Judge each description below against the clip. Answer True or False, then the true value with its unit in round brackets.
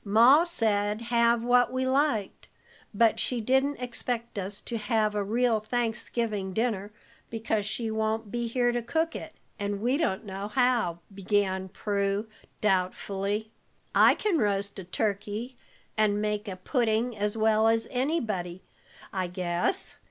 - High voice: True (220 Hz)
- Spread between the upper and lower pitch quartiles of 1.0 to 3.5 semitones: True (3.0 semitones)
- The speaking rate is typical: True (145 wpm)